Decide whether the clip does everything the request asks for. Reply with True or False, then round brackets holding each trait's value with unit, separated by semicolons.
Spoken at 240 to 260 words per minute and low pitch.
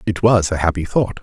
True (245 wpm; 95 Hz)